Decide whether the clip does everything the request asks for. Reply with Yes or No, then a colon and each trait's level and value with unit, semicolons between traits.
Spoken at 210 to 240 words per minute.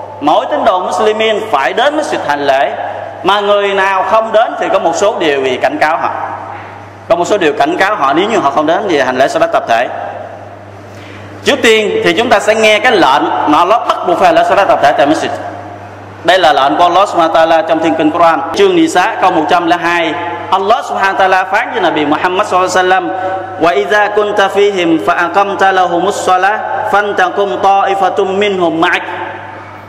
No: average, 195 wpm